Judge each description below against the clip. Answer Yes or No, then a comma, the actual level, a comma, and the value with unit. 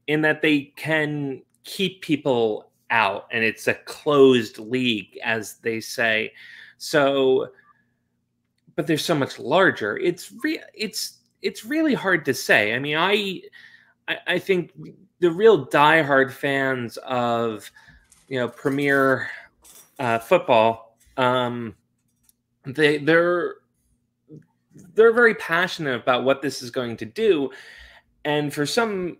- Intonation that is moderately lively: No, wide, 6.6 semitones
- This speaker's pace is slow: Yes, slow, 125 wpm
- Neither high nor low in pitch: Yes, medium, 145 Hz